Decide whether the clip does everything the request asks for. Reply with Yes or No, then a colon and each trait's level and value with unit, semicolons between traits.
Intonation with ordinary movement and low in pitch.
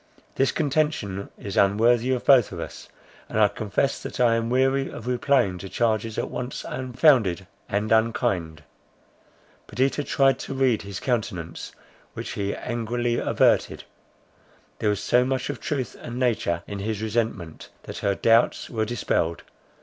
Yes: average, 4.1 semitones; low, 115 Hz